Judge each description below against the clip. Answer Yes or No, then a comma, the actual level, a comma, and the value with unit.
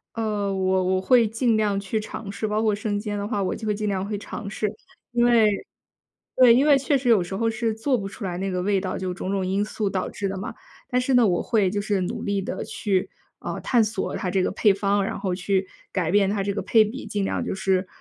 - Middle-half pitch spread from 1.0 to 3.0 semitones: Yes, narrow, 2.5 semitones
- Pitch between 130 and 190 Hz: No, high, 205 Hz